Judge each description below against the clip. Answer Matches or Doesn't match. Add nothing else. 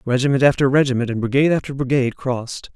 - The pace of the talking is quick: Doesn't match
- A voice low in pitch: Matches